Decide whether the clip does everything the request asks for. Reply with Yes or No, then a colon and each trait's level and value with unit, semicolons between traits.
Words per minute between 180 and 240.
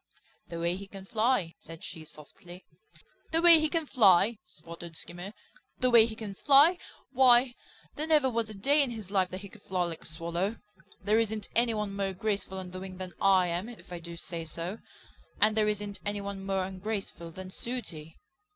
Yes: average, 200 wpm